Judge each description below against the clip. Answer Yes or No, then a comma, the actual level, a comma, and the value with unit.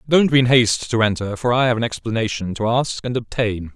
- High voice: No, low, 115 Hz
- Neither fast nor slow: No, fast, 240 wpm